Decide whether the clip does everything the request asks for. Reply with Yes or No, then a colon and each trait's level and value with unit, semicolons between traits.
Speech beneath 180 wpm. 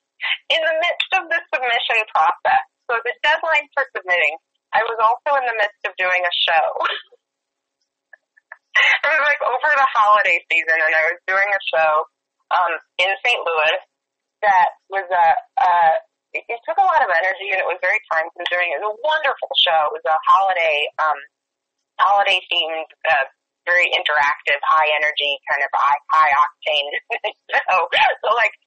Yes: average, 165 wpm